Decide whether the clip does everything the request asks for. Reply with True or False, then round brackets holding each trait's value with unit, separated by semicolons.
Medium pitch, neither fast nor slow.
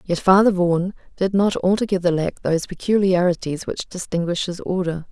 True (180 Hz; 155 wpm)